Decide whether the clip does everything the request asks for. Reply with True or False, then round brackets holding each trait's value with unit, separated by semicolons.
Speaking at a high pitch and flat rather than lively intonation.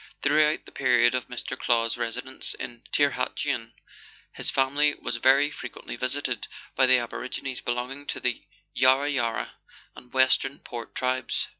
False (130 Hz; 2.3 semitones)